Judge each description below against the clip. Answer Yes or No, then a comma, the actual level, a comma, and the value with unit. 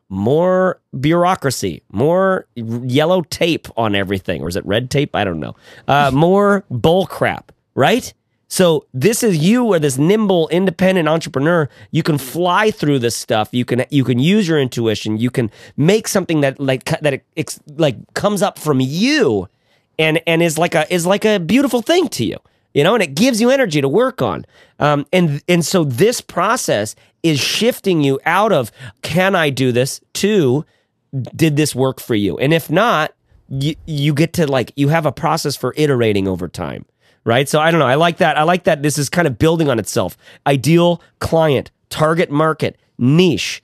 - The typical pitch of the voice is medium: Yes, medium, 150 Hz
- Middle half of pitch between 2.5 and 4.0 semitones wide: No, wide, 5.6 semitones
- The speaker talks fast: No, average, 190 wpm